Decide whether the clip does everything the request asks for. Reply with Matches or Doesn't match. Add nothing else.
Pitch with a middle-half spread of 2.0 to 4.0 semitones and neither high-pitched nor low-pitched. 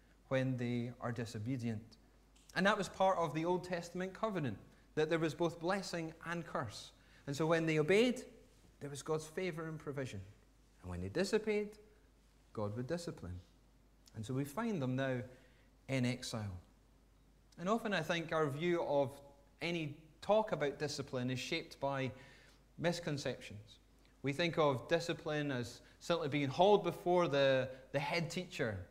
Doesn't match